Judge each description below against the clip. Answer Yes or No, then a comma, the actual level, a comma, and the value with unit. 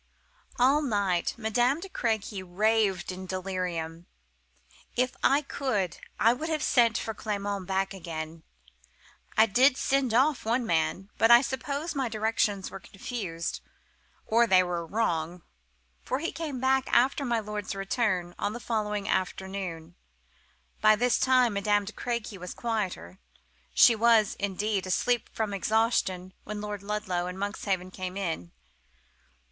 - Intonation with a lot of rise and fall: No, average, 4.2 semitones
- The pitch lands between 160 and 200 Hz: No, high, 210 Hz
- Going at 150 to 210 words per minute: No, average, 140 wpm